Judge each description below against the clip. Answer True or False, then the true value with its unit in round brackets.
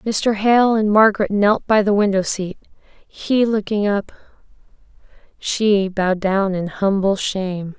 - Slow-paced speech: True (130 wpm)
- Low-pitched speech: False (205 Hz)